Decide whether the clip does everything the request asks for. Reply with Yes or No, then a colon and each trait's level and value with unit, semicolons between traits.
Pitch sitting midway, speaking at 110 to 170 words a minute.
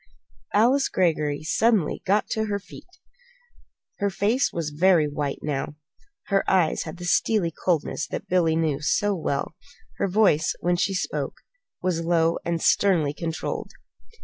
Yes: medium, 175 Hz; average, 145 wpm